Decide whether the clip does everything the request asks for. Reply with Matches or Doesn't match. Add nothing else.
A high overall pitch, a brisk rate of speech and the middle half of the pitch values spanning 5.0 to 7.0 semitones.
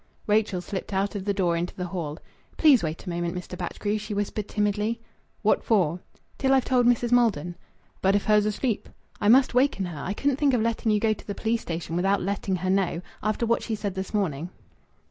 Doesn't match